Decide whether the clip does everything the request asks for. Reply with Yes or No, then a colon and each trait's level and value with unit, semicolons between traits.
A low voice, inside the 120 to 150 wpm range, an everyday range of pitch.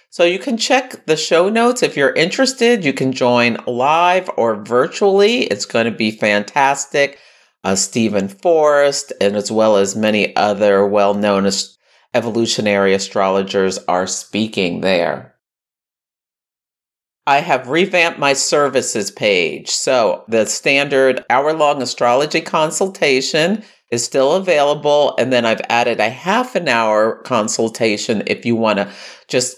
No: low, 120 Hz; average, 140 wpm; wide, 6.9 semitones